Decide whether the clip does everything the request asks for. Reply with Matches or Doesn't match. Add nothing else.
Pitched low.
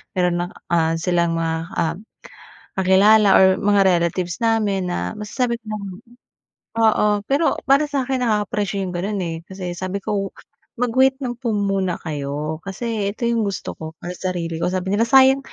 Doesn't match